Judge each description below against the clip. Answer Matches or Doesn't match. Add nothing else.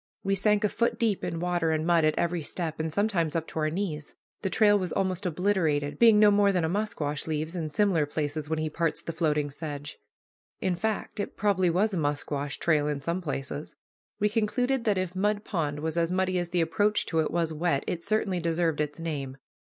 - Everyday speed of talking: Doesn't match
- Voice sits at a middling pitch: Matches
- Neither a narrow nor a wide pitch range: Matches